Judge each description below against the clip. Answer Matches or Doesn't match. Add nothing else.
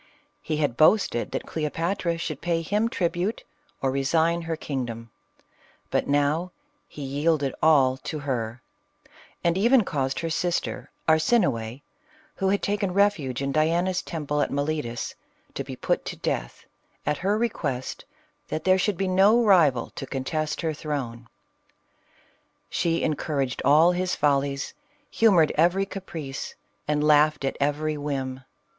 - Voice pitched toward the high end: Doesn't match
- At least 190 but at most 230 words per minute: Doesn't match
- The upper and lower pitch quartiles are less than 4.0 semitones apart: Doesn't match